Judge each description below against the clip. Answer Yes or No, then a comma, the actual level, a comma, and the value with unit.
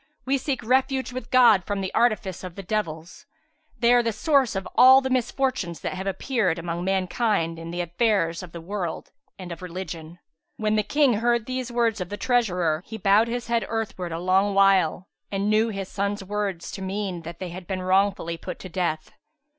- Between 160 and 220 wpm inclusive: Yes, average, 200 wpm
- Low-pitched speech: No, high, 195 Hz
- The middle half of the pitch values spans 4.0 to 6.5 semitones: Yes, average, 4.6 semitones